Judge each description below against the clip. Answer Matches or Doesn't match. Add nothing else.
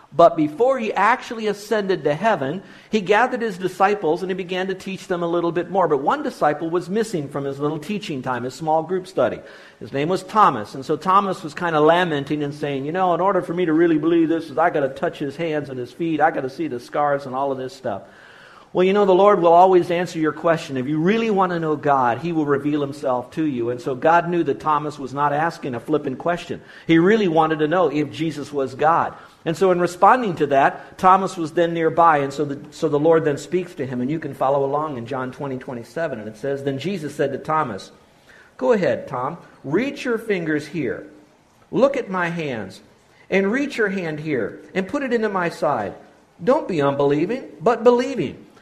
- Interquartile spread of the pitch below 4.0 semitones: Doesn't match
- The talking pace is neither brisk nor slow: Doesn't match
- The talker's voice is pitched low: Doesn't match